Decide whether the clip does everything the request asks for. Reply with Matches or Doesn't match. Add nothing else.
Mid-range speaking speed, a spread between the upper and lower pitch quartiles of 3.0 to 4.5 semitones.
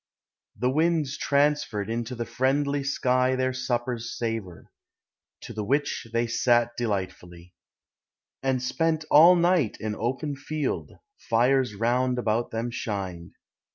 Doesn't match